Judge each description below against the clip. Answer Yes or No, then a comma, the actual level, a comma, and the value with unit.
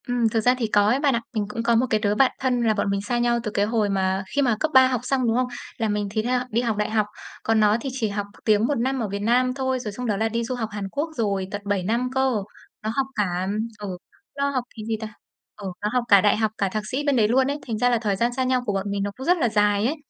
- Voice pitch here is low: No, high, 225 Hz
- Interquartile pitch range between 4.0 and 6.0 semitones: No, average, 3.4 semitones